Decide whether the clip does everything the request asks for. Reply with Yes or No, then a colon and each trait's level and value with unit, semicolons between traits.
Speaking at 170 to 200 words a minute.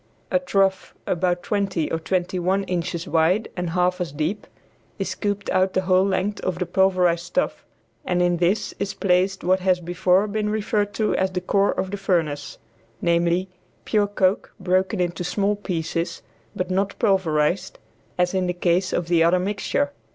Yes: average, 175 wpm